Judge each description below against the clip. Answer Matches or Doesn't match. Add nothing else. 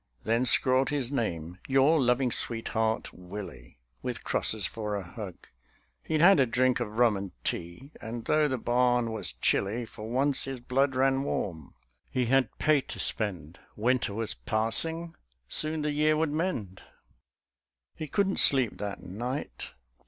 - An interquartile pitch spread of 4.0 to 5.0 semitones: Matches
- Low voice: Matches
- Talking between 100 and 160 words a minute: Matches